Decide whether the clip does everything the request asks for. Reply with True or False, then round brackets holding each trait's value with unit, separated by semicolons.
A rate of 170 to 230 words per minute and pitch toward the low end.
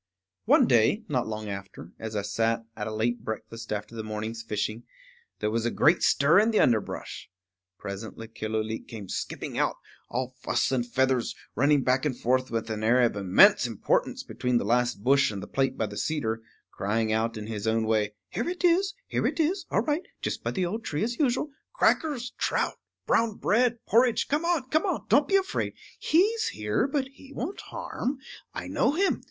True (195 wpm; 120 Hz)